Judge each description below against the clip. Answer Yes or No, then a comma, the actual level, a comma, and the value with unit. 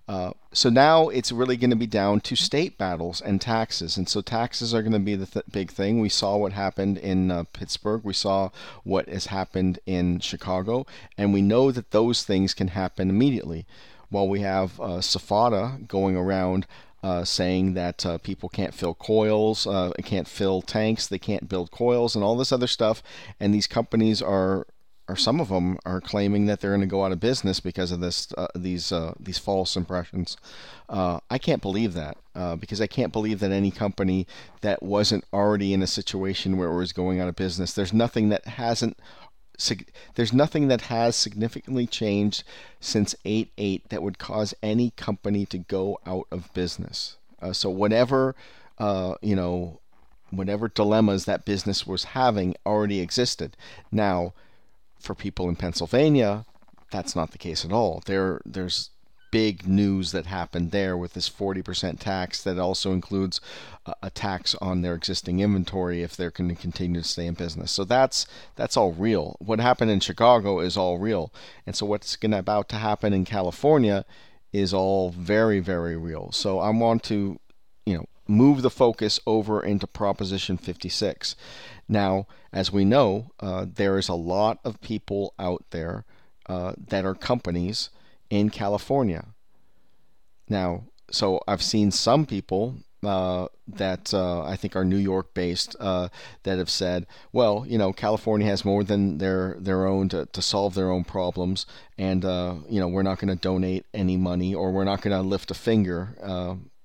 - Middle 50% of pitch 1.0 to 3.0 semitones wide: Yes, average, 2.7 semitones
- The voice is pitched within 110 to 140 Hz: No, very low, 95 Hz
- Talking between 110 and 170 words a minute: No, average, 180 wpm